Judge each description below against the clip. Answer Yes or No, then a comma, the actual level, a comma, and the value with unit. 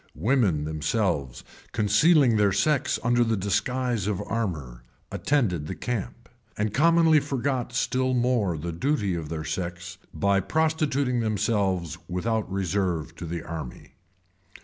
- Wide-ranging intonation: Yes, wide, 6.6 semitones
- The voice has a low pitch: Yes, low, 105 Hz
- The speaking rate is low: Yes, slow, 125 wpm